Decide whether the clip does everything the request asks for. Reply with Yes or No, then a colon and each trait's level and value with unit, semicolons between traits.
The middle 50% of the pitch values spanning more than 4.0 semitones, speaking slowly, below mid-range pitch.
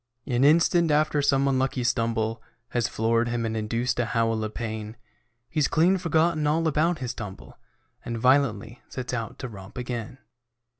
No: average, 4.6 semitones; average, 160 wpm; low, 125 Hz